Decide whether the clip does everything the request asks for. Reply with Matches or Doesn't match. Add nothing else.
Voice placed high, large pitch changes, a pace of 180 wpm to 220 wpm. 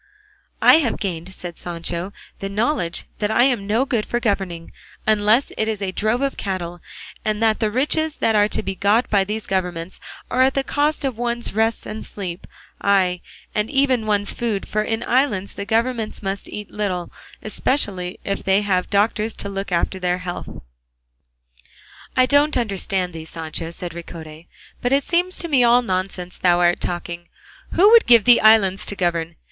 Doesn't match